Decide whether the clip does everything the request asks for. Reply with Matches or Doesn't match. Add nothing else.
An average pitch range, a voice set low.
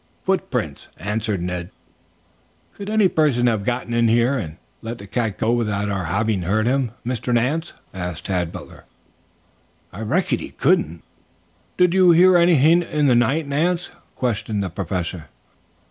Doesn't match